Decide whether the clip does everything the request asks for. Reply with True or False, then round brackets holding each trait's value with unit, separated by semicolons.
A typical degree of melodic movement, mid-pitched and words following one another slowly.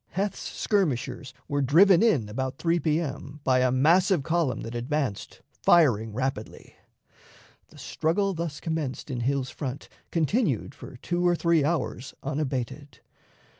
True (4.7 semitones; 145 Hz; 130 wpm)